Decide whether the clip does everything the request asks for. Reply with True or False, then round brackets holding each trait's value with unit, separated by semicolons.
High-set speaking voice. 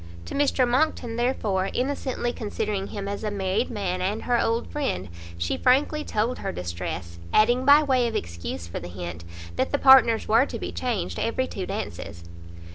True (215 Hz)